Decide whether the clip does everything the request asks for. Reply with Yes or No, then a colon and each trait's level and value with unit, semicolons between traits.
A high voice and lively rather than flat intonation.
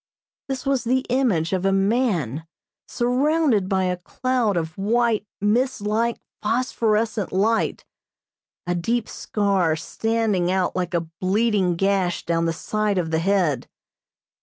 No: high, 205 Hz; average, 4.6 semitones